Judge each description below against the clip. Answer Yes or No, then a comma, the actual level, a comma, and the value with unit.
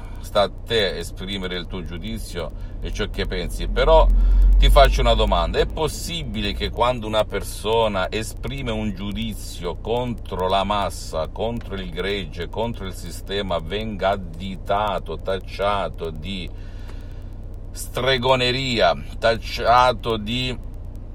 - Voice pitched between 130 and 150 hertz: No, very low, 95 Hz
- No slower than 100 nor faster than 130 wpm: Yes, slow, 115 wpm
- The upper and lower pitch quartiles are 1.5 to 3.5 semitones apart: Yes, average, 3.2 semitones